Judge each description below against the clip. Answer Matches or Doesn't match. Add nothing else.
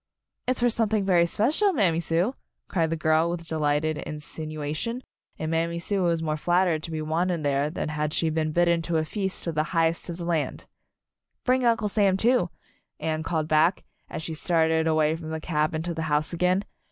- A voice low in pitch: Doesn't match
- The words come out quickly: Matches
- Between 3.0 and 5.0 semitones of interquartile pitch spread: Doesn't match